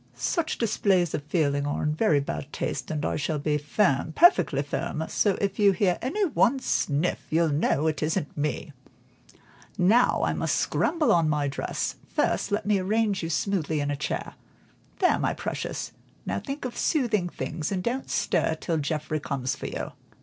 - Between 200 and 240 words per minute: No, average, 185 wpm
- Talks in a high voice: No, medium, 165 Hz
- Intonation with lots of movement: Yes, wide, 5.9 semitones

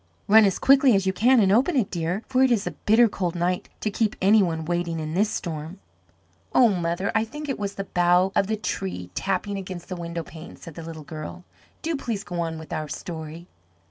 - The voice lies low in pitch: No, medium, 185 Hz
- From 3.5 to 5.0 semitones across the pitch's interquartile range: Yes, average, 4.4 semitones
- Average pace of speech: No, fast, 225 wpm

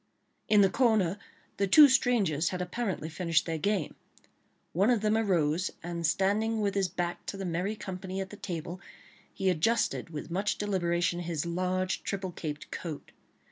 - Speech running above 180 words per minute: No, average, 165 wpm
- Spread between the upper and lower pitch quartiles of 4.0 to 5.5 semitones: No, average, 3.2 semitones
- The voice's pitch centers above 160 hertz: Yes, medium, 185 Hz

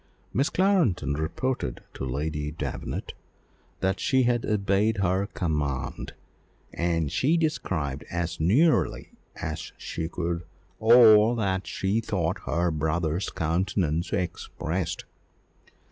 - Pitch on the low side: Yes, very low, 90 Hz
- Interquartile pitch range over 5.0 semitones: Yes, wide, 5.4 semitones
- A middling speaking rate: No, slow, 105 wpm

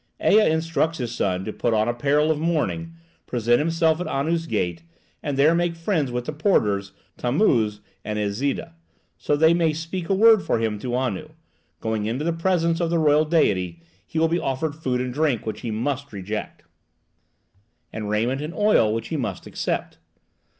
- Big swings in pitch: Yes, wide, 6.5 semitones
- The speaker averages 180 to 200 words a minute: Yes, average, 185 wpm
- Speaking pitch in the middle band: Yes, medium, 145 Hz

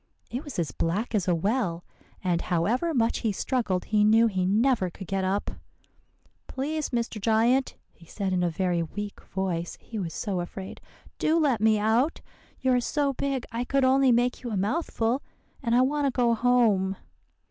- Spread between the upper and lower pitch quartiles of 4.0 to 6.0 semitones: Yes, average, 5.0 semitones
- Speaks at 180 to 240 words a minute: Yes, average, 185 wpm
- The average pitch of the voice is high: Yes, high, 225 Hz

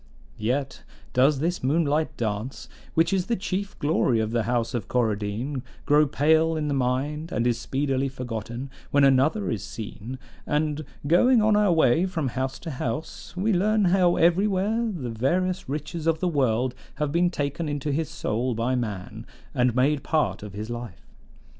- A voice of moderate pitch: Yes, medium, 145 Hz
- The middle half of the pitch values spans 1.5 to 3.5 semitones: No, wide, 5.5 semitones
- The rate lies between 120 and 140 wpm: No, average, 170 wpm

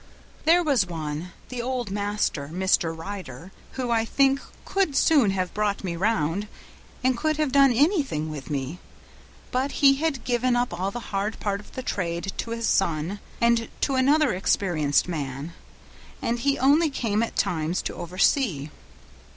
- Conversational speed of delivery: Yes, average, 160 wpm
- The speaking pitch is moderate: No, high, 210 Hz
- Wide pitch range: Yes, wide, 7.1 semitones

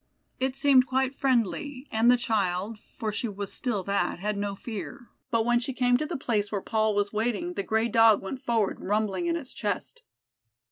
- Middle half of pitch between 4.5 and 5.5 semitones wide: No, average, 3.8 semitones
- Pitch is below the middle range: No, high, 225 Hz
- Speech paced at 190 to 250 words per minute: Yes, average, 195 wpm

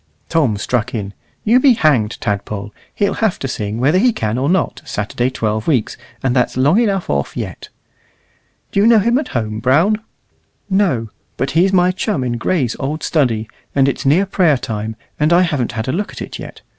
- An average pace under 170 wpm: No, average, 195 wpm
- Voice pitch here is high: No, low, 135 Hz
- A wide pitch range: Yes, wide, 8.6 semitones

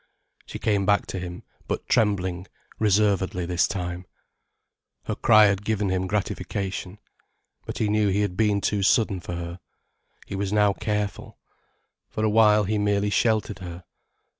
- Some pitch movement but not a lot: No, narrow, 2.1 semitones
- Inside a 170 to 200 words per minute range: No, average, 155 wpm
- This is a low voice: Yes, low, 100 Hz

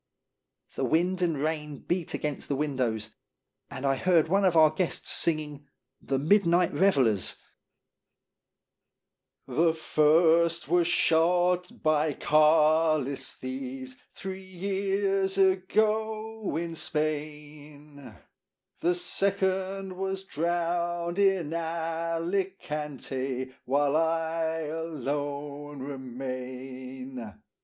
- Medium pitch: Yes, medium, 160 Hz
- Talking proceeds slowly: Yes, slow, 95 wpm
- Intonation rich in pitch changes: No, average, 3.9 semitones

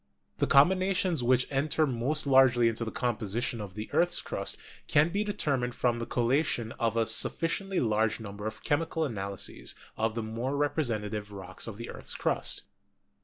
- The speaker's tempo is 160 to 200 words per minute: Yes, average, 170 wpm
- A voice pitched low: Yes, low, 120 Hz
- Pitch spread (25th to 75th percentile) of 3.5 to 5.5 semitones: Yes, average, 4.9 semitones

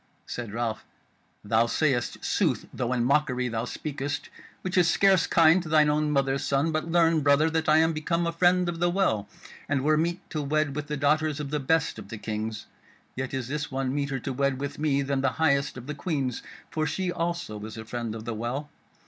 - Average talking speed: No, fast, 215 wpm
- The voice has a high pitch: No, medium, 145 Hz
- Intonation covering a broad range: No, average, 3.9 semitones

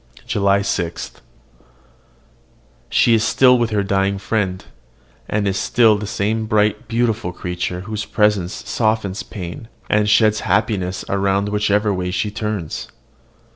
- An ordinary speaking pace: No, slow, 130 wpm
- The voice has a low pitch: Yes, low, 105 Hz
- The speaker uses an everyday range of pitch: No, narrow, 2.0 semitones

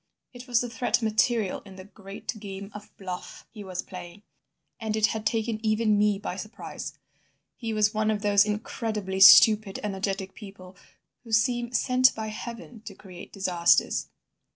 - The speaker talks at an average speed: Yes, average, 160 wpm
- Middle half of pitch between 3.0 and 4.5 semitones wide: No, narrow, 2.4 semitones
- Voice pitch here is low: No, high, 210 Hz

